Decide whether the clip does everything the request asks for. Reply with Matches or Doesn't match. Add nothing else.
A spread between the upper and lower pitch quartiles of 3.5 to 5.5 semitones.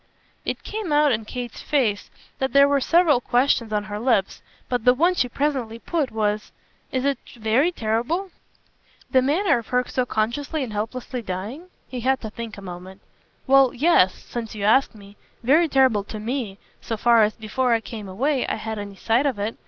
Matches